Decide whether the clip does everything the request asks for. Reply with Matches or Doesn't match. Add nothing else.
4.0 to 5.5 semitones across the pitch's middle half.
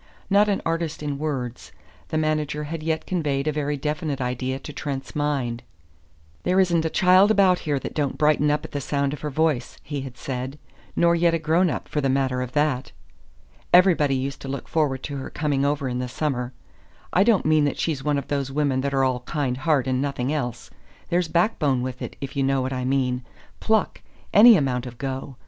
Doesn't match